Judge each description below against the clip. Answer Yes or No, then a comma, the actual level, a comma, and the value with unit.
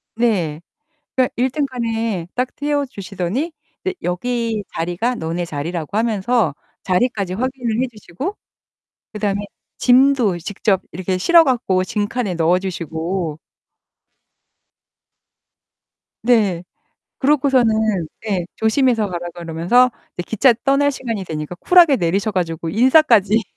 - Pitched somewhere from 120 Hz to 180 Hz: No, high, 215 Hz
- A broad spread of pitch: Yes, wide, 6.1 semitones